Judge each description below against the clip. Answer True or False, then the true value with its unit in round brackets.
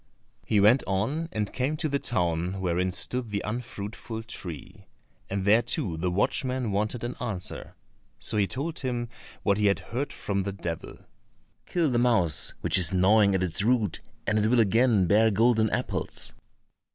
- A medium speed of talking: True (170 wpm)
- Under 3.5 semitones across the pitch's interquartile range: False (4.2 semitones)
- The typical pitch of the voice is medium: False (105 Hz)